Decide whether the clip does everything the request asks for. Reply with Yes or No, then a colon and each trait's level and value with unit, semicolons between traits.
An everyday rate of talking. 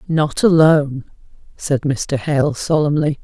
No: slow, 110 wpm